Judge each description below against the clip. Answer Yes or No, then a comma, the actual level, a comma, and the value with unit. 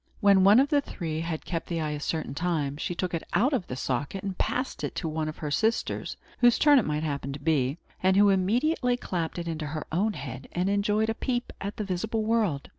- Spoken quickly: Yes, fast, 240 wpm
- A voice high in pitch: No, medium, 180 Hz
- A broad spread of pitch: Yes, wide, 5.8 semitones